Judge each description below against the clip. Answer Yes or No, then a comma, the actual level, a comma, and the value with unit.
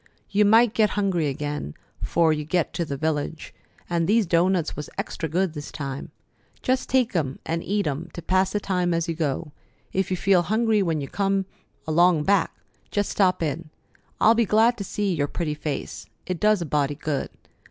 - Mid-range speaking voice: Yes, medium, 170 Hz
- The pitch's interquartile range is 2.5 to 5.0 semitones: Yes, average, 4.7 semitones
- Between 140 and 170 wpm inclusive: No, average, 195 wpm